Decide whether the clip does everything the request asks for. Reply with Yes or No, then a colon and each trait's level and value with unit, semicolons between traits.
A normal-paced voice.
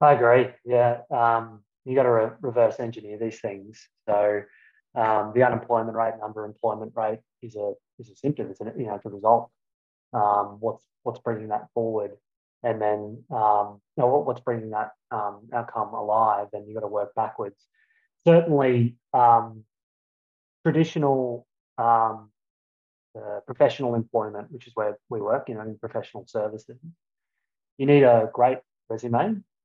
Yes: average, 155 wpm